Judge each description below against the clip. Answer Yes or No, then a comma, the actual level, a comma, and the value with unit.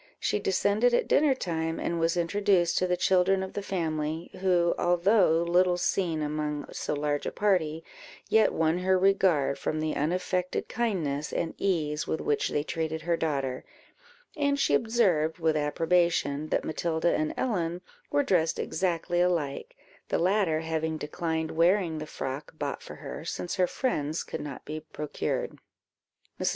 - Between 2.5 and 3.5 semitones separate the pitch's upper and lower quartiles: Yes, average, 3.1 semitones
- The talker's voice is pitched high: No, medium, 165 Hz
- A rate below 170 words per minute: Yes, average, 160 wpm